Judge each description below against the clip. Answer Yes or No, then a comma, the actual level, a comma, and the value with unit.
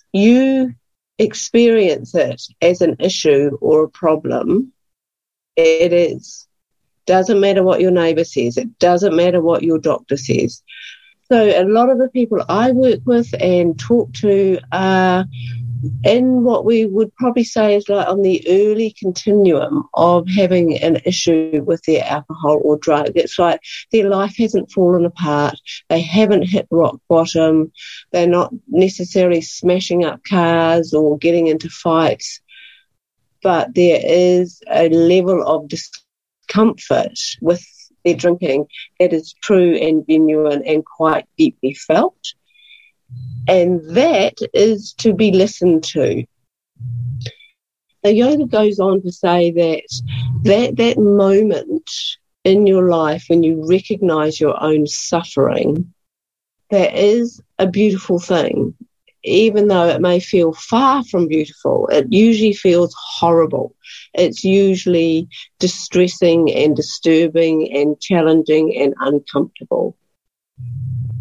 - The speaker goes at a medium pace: No, slow, 130 wpm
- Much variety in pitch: No, average, 4.6 semitones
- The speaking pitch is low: No, medium, 180 Hz